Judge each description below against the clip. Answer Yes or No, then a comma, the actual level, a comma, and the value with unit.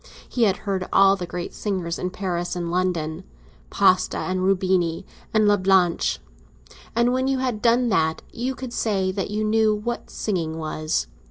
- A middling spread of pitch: Yes, average, 3.6 semitones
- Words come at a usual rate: Yes, average, 155 wpm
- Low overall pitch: No, high, 190 Hz